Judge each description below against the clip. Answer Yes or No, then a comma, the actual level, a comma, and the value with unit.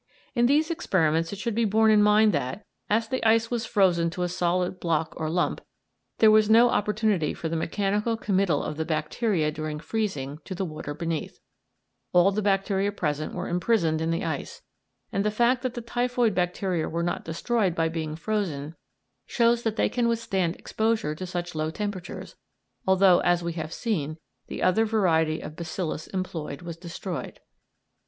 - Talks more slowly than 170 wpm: No, average, 175 wpm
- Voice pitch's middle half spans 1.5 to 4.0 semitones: No, average, 5.0 semitones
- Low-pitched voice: No, medium, 185 Hz